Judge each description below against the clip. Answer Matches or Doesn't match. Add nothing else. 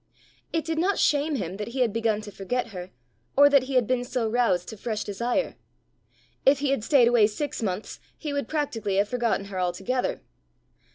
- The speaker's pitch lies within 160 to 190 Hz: Doesn't match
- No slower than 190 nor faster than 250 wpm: Matches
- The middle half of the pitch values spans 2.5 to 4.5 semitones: Doesn't match